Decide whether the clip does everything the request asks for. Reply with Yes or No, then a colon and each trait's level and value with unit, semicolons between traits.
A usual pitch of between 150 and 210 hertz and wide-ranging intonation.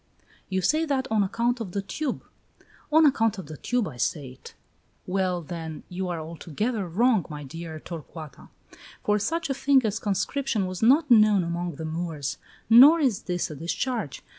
Yes: high, 190 Hz; wide, 6.6 semitones